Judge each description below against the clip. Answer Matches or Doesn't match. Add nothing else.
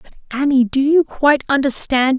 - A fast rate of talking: Doesn't match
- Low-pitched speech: Doesn't match